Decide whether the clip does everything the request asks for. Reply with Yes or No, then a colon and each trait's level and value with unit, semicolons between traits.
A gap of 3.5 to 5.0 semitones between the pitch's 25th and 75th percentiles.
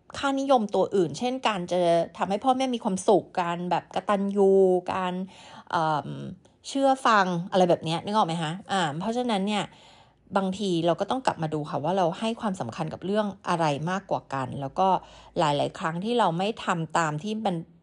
Yes: average, 4.0 semitones